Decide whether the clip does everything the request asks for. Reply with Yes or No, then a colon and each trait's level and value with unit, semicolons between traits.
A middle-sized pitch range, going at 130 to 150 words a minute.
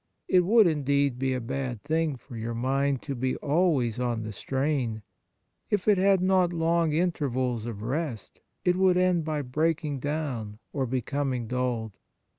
No: average, 5.0 semitones; average, 160 wpm